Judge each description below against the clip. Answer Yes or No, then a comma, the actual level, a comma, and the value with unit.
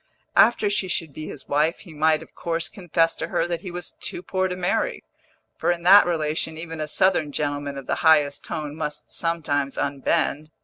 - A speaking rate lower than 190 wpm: No, average, 200 wpm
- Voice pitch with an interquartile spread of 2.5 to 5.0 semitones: Yes, average, 2.8 semitones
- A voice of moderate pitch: Yes, medium, 160 Hz